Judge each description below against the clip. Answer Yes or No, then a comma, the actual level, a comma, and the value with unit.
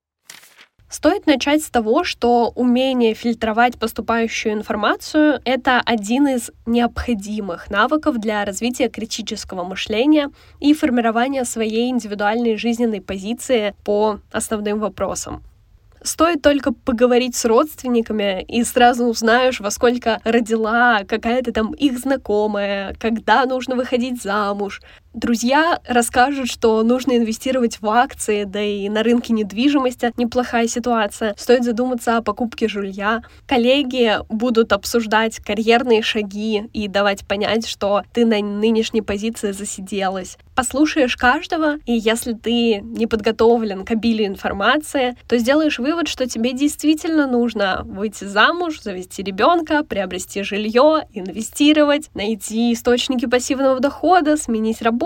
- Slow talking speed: No, average, 120 wpm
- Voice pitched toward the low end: No, high, 235 Hz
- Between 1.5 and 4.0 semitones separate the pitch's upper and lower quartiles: Yes, average, 2.9 semitones